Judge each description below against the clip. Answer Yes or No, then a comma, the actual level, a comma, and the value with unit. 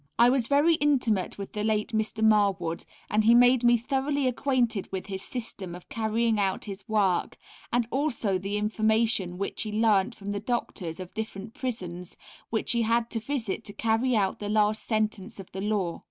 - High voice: Yes, high, 220 Hz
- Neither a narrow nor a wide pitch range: Yes, average, 3.1 semitones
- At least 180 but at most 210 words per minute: Yes, average, 185 wpm